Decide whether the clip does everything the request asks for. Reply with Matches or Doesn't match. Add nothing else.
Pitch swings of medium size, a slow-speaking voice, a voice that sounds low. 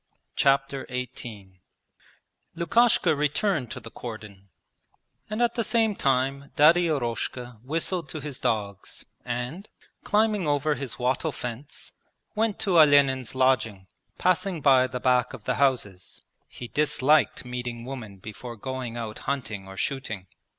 Matches